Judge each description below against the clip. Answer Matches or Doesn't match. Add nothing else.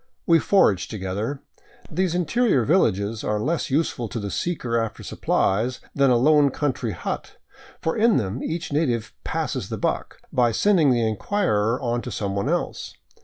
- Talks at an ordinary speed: Matches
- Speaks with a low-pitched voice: Matches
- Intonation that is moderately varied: Doesn't match